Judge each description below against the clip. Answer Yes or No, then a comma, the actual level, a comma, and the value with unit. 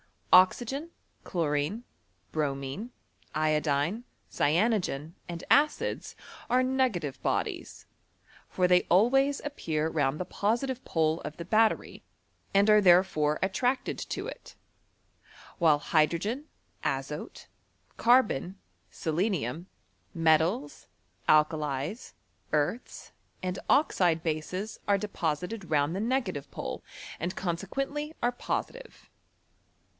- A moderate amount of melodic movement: No, wide, 6.7 semitones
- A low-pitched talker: No, medium, 180 Hz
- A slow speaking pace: Yes, slow, 100 wpm